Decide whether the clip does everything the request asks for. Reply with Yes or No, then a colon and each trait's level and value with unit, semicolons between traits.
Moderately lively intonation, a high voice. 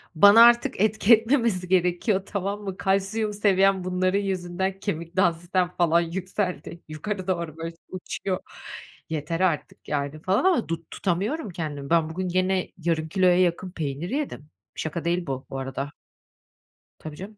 No: average, 3.0 semitones; medium, 180 Hz